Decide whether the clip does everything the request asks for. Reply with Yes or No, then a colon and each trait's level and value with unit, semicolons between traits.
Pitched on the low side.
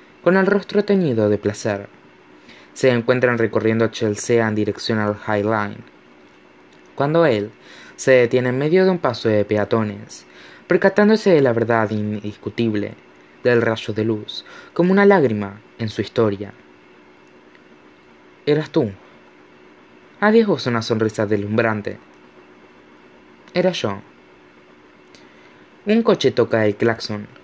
Yes: low, 110 Hz